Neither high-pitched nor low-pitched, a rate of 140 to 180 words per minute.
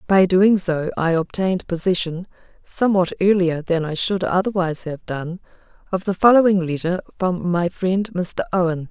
Yes: medium, 180 Hz; average, 155 wpm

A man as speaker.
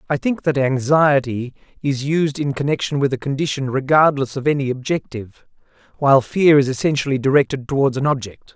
Yes: male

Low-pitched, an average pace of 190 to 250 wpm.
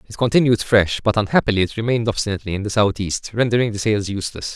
Yes: low, 105 Hz; average, 200 wpm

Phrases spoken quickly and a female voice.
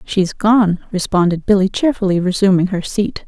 No: average, 145 wpm; female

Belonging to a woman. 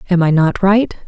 Yes: female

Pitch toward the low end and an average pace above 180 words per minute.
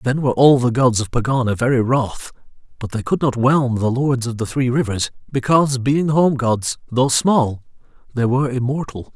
Yes: low, 125 Hz; average, 190 wpm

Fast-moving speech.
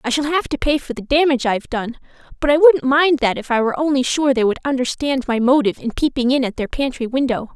Yes: fast, 255 wpm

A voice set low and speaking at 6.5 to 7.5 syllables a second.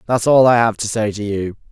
No: low, 110 Hz; 5.6 syllables/s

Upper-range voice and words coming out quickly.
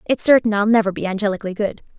Yes: high, 210 Hz; fast, 210 wpm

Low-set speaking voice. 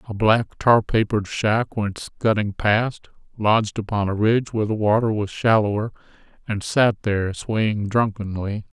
Yes: low, 105 Hz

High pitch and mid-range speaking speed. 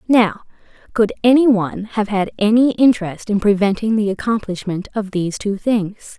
Yes: high, 210 Hz; average, 155 wpm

